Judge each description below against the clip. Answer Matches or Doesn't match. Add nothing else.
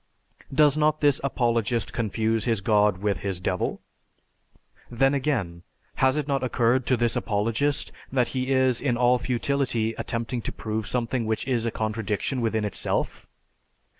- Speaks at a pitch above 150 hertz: Doesn't match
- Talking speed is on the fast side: Doesn't match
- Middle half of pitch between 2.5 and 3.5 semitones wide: Matches